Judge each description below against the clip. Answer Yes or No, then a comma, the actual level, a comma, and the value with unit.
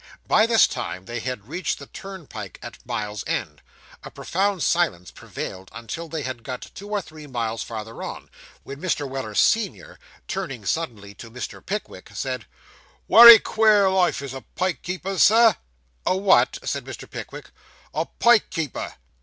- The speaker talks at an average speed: Yes, average, 160 wpm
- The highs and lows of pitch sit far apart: Yes, wide, 8.9 semitones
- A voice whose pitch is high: No, medium, 155 Hz